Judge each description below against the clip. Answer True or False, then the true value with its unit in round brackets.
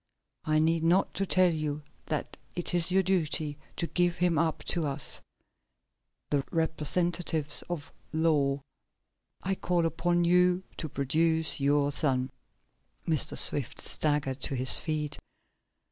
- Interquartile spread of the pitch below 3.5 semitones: True (3.1 semitones)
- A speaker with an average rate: False (130 wpm)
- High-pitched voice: False (160 Hz)